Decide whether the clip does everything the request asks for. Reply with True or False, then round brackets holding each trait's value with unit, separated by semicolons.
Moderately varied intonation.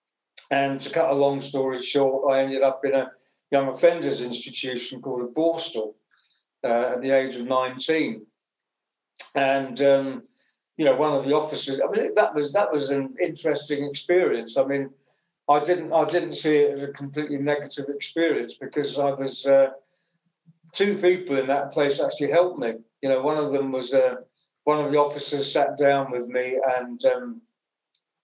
False (2.3 semitones)